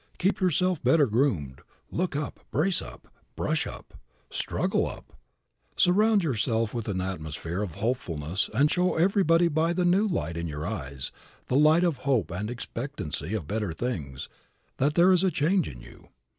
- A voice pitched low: Yes, low, 130 Hz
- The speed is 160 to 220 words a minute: Yes, average, 165 wpm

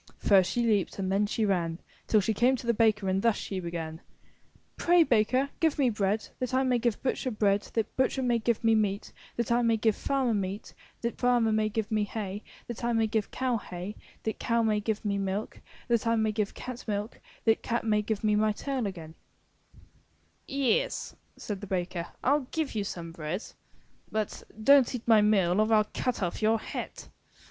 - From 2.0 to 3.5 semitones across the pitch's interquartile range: Yes, average, 2.9 semitones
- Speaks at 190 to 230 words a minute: Yes, fast, 205 wpm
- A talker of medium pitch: No, high, 220 Hz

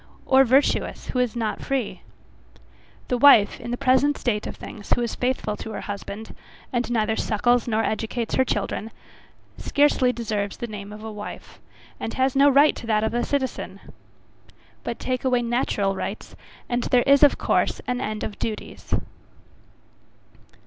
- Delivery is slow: No, average, 165 wpm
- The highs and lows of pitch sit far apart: No, average, 3.2 semitones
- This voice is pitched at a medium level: No, high, 240 Hz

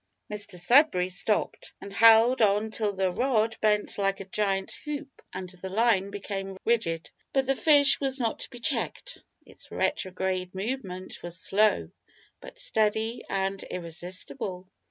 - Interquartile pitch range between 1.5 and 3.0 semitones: No, average, 3.6 semitones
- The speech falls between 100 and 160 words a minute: Yes, average, 145 wpm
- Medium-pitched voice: No, high, 205 Hz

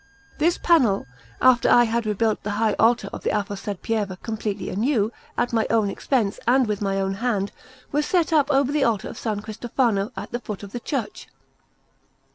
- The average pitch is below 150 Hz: No, high, 225 Hz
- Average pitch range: Yes, average, 3.7 semitones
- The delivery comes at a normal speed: Yes, average, 190 wpm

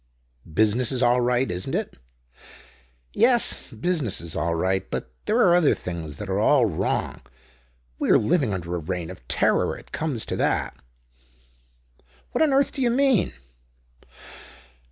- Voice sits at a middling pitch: No, low, 110 Hz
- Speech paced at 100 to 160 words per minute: Yes, average, 155 wpm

